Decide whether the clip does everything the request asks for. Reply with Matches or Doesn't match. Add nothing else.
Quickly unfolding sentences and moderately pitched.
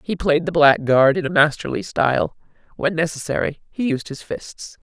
Doesn't match